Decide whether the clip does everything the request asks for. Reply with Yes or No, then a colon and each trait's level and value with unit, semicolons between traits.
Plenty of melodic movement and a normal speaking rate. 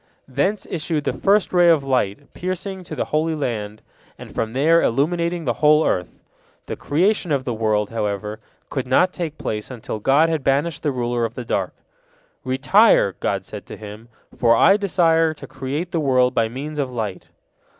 Yes: wide, 6.2 semitones; average, 180 wpm